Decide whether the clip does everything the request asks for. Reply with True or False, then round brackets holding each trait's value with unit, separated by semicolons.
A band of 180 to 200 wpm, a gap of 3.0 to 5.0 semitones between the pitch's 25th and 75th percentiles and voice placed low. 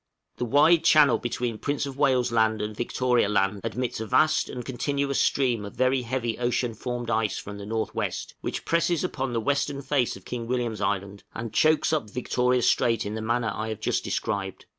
True (195 wpm; 3.4 semitones; 120 Hz)